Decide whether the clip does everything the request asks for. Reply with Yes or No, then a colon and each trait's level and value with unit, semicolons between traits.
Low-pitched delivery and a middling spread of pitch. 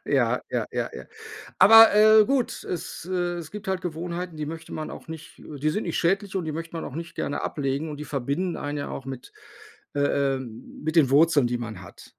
No: medium, 160 Hz; average, 4.0 semitones